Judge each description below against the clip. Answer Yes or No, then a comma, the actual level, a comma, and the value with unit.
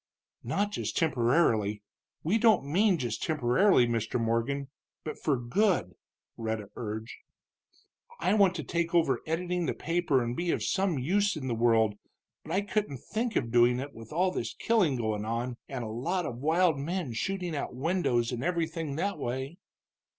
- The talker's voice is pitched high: No, medium, 145 Hz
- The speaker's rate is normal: Yes, average, 170 wpm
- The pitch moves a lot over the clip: Yes, wide, 7.0 semitones